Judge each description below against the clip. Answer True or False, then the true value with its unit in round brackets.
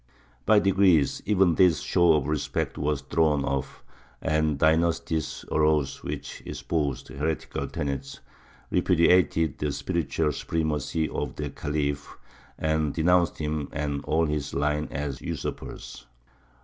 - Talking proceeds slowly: True (120 wpm)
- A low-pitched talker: True (75 Hz)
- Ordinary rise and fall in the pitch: False (2.3 semitones)